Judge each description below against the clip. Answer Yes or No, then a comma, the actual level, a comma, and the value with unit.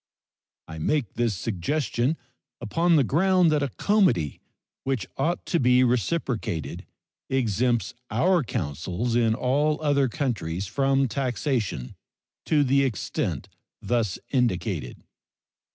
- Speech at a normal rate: No, slow, 110 wpm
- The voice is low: Yes, low, 125 Hz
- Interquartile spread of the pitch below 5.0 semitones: No, average, 5.3 semitones